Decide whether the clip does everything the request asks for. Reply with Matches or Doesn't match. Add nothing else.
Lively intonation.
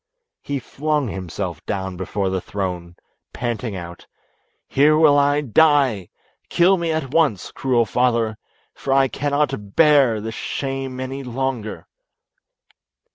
Matches